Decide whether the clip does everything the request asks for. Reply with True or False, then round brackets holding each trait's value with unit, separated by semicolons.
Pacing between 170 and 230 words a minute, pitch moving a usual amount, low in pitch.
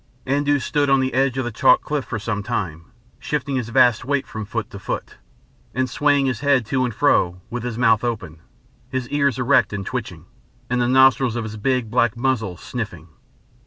True (200 wpm; 3.5 semitones; 125 Hz)